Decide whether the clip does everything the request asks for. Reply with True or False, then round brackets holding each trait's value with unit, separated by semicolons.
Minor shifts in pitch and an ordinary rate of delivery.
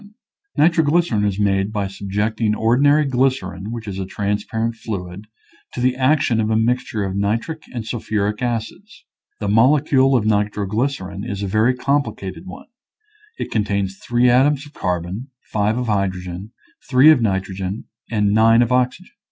False (4.0 semitones; 155 wpm)